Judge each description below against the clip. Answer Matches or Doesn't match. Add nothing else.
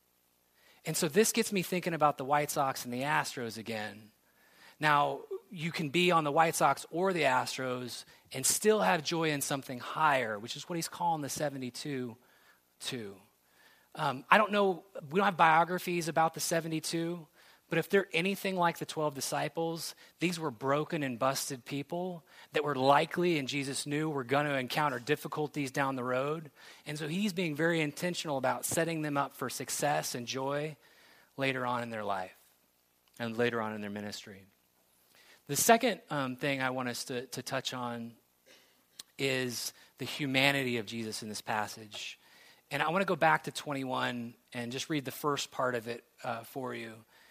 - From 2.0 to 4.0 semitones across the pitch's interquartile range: Doesn't match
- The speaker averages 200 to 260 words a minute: Doesn't match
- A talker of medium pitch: Matches